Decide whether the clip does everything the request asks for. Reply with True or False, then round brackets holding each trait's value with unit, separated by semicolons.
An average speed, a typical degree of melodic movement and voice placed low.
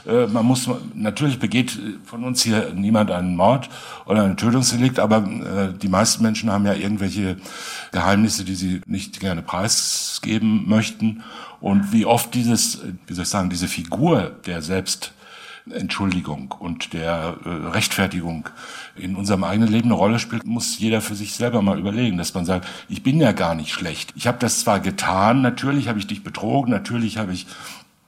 True (165 wpm; 3.5 semitones; 105 Hz)